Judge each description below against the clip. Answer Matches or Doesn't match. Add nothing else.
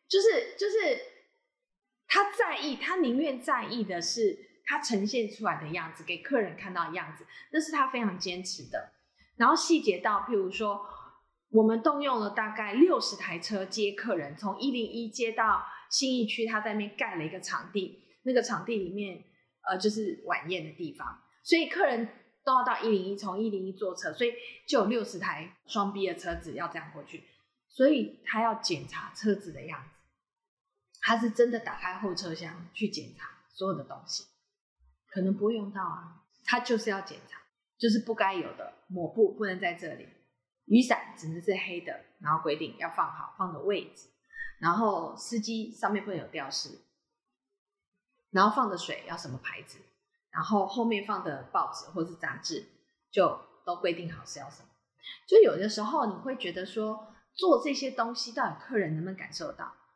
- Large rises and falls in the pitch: Matches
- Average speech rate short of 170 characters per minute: Doesn't match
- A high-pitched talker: Matches